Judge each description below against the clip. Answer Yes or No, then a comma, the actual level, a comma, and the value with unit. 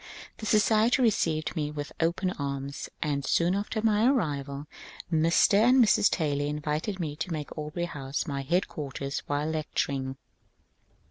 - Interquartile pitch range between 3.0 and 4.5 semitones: No, average, 5.2 semitones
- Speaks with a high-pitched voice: No, medium, 155 Hz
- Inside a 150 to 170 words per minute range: No, average, 140 wpm